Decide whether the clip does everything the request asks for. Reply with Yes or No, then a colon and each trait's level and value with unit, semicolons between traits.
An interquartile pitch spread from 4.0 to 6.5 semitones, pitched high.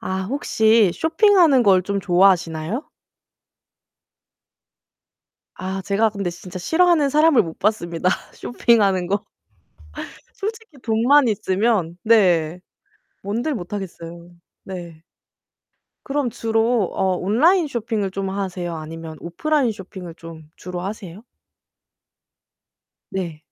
Yes: average, 5.1 semitones; high, 200 Hz